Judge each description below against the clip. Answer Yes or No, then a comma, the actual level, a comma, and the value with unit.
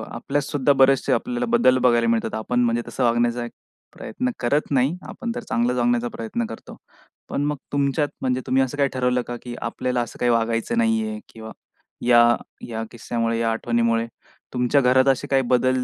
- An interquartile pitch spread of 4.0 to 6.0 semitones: No, average, 2.7 semitones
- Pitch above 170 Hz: No, low, 125 Hz